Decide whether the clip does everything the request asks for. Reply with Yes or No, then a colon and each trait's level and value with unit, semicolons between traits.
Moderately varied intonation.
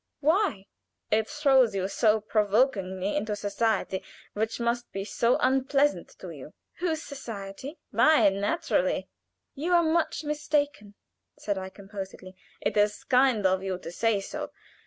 No: wide, 6.3 semitones